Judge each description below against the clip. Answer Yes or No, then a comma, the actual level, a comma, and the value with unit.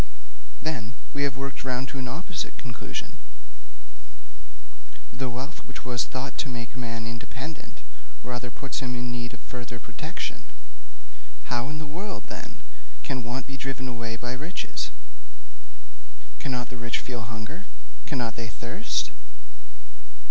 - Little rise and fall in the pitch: Yes, narrow, 2.3 semitones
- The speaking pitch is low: Yes, low, 125 Hz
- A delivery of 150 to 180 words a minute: No, average, 140 wpm